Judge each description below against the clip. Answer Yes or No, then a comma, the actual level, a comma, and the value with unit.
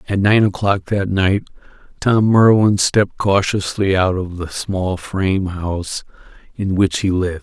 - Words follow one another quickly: No, average, 155 wpm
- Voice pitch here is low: Yes, very low, 95 Hz